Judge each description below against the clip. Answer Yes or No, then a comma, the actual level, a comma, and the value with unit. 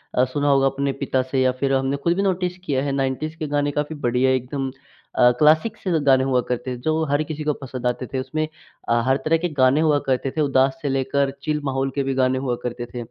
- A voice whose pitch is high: No, low, 135 Hz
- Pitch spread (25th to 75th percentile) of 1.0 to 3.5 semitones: Yes, narrow, 2.5 semitones